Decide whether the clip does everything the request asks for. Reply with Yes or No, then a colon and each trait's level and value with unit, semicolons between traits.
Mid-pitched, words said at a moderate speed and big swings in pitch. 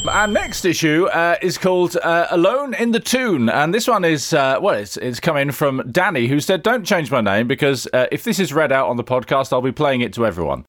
No: medium, 150 Hz; fast, 245 wpm; wide, 6.1 semitones